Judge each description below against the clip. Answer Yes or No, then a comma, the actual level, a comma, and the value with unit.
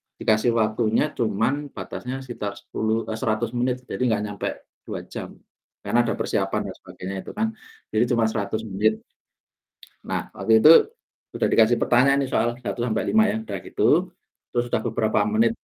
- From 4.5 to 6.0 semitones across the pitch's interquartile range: No, average, 2.8 semitones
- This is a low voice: Yes, low, 120 Hz